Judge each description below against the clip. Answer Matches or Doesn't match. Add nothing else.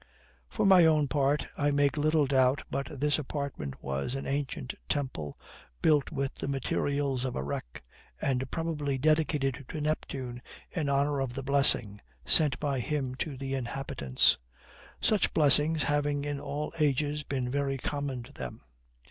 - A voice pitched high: Doesn't match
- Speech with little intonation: Matches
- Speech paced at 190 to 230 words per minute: Doesn't match